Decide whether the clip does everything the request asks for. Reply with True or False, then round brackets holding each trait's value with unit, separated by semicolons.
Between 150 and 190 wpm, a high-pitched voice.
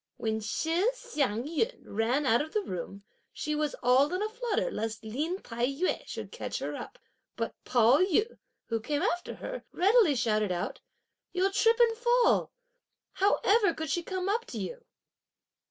True (170 wpm; 320 Hz)